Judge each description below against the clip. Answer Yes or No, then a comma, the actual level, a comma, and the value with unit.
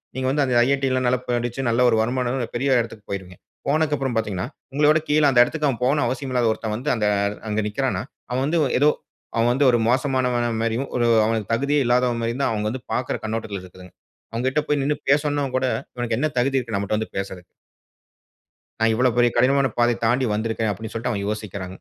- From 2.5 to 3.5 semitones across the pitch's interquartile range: Yes, average, 3.2 semitones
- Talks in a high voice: No, low, 120 Hz